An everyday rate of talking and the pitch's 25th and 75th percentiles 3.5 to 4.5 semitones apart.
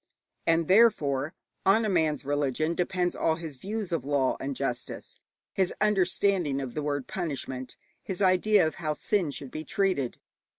No: average, 160 wpm; average, 5.1 semitones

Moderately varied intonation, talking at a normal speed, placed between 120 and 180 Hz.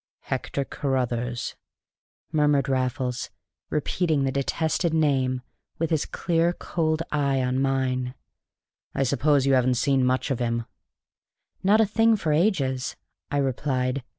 No: average, 3.5 semitones; slow, 125 wpm; low, 135 Hz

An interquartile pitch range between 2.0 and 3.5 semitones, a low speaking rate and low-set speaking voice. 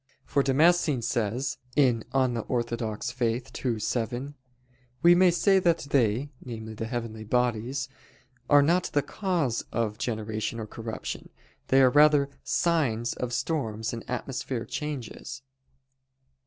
No: average, 4.0 semitones; slow, 120 wpm; low, 125 Hz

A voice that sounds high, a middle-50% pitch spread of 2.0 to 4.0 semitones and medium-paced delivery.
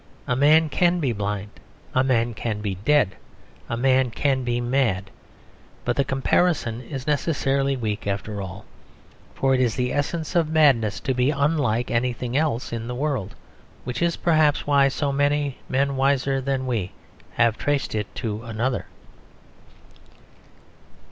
No: low, 130 Hz; average, 3.7 semitones; average, 150 wpm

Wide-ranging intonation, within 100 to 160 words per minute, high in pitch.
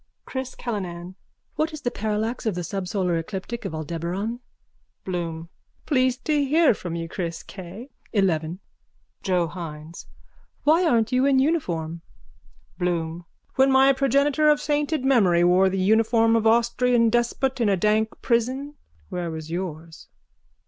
Yes: wide, 7.0 semitones; average, 145 wpm; high, 215 Hz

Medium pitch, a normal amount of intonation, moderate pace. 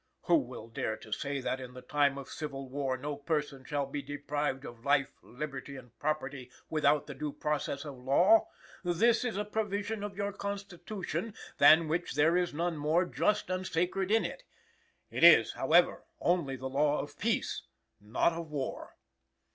Yes: medium, 150 Hz; average, 4.9 semitones; average, 170 wpm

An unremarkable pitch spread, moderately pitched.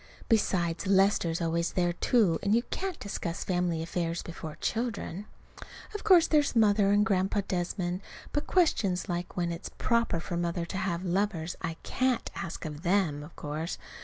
Yes: average, 3.6 semitones; medium, 180 Hz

